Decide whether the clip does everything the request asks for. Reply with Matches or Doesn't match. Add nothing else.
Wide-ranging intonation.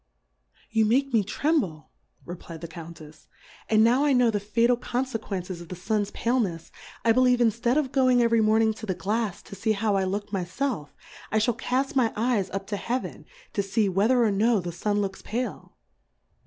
Doesn't match